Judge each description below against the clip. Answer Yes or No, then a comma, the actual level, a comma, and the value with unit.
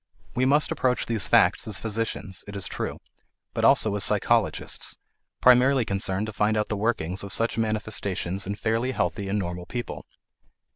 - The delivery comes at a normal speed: Yes, average, 165 wpm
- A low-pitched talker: Yes, low, 105 Hz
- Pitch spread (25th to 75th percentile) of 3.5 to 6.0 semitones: No, average, 2.8 semitones